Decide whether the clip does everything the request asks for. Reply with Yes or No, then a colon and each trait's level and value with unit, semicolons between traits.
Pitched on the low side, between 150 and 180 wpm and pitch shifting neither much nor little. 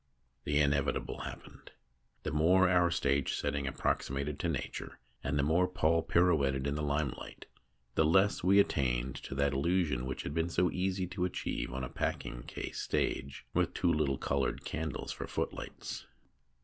Yes: very low, 75 Hz; average, 160 wpm; average, 4.1 semitones